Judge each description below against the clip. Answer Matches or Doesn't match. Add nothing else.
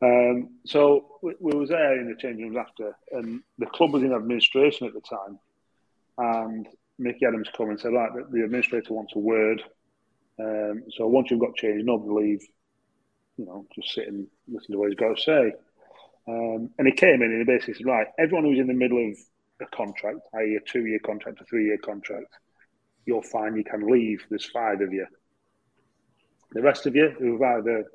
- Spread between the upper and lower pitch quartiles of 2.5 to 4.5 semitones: Matches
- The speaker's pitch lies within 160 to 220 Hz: Doesn't match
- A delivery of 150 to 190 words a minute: Doesn't match